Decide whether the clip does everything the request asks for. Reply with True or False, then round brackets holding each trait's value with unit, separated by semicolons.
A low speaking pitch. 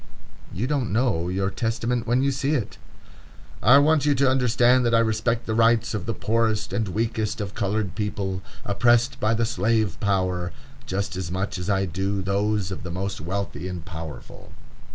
True (105 Hz)